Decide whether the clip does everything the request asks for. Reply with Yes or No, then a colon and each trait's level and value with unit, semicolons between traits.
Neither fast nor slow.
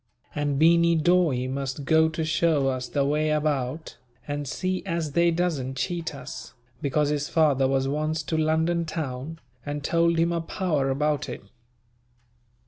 Yes: average, 155 wpm